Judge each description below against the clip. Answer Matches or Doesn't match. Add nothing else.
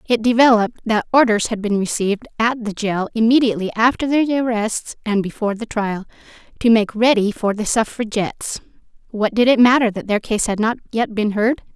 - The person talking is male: Doesn't match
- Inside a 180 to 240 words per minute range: Matches